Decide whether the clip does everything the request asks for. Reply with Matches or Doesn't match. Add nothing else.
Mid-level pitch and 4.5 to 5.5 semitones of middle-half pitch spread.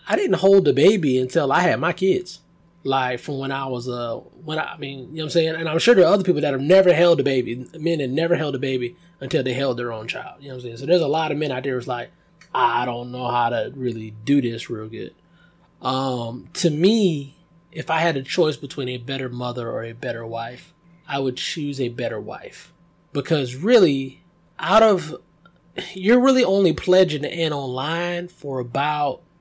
Matches